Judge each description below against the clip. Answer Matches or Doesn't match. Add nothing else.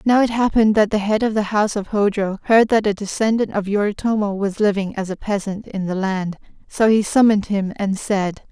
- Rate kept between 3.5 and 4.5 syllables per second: Doesn't match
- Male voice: Doesn't match